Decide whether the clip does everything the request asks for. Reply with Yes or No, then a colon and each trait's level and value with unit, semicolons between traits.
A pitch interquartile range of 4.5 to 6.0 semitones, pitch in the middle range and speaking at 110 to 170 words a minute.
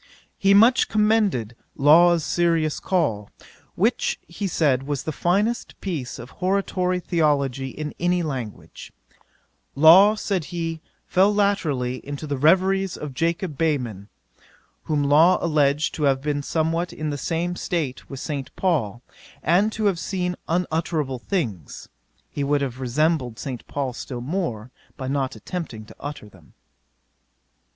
Yes: average, 4.9 semitones; medium, 155 Hz; average, 140 wpm